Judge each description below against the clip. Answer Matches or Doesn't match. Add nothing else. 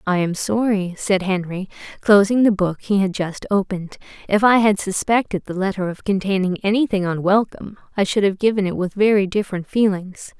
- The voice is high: Matches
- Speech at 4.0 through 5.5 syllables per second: Matches